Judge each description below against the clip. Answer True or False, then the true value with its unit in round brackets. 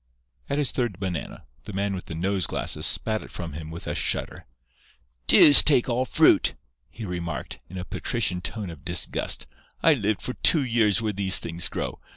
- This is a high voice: False (100 Hz)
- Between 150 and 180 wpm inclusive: False (190 wpm)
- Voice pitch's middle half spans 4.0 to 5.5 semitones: True (5.0 semitones)